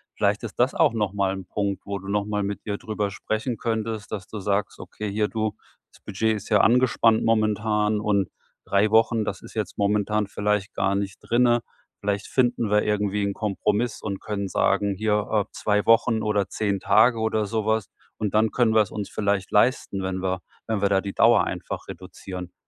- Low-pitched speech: Yes, low, 105 Hz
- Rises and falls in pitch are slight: Yes, narrow, 1.6 semitones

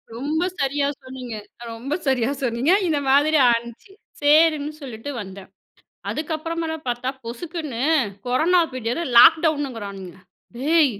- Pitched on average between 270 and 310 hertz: Yes, very high, 275 Hz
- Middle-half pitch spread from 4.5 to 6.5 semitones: Yes, average, 4.8 semitones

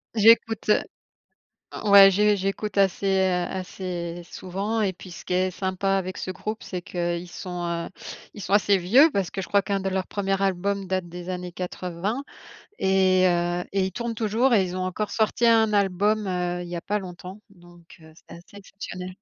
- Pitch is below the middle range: No, high, 190 Hz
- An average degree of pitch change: No, narrow, 2.1 semitones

